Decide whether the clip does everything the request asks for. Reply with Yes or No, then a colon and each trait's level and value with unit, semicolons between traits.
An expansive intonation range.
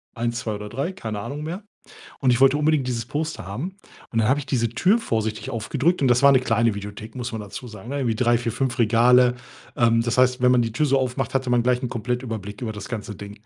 No: average, 2.9 semitones